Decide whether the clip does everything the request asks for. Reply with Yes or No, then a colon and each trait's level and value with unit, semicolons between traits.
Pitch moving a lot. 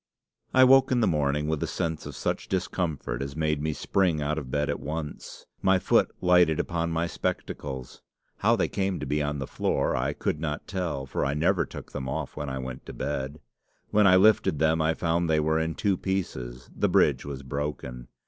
No: average, 3.5 semitones